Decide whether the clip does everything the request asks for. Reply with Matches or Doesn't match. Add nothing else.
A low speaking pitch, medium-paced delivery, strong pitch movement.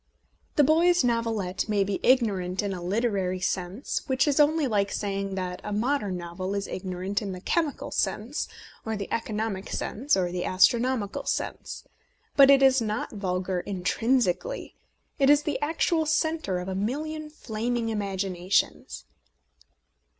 Doesn't match